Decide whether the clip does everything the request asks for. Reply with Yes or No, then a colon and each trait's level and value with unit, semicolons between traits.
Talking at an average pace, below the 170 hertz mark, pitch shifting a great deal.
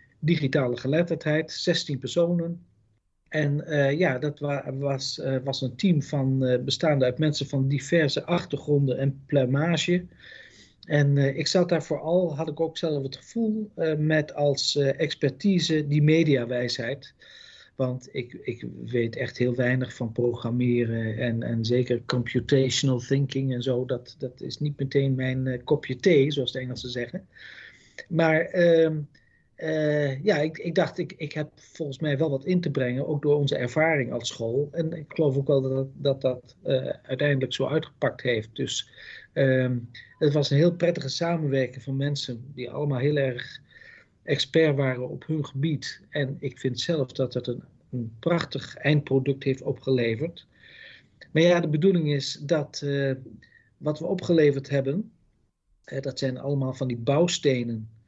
No: average, 160 wpm; medium, 140 Hz; average, 3.4 semitones